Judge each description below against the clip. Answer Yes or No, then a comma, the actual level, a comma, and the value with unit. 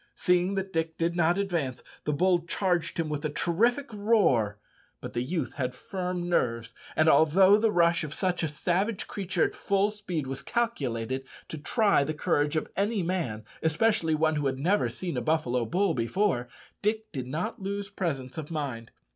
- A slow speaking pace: No, average, 180 wpm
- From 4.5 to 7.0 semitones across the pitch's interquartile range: Yes, wide, 5.4 semitones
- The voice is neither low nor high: Yes, medium, 165 Hz